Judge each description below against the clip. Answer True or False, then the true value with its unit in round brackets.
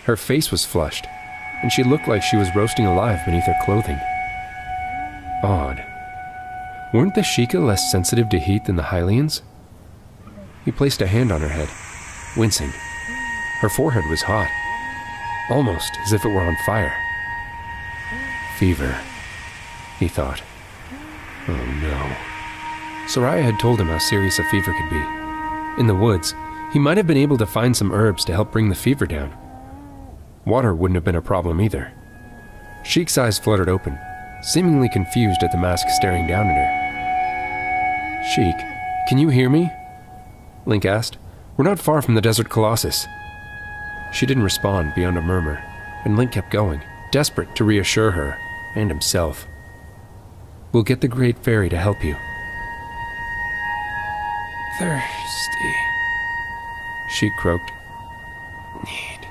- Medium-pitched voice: False (105 Hz)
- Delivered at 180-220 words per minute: False (140 wpm)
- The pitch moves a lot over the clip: True (5.9 semitones)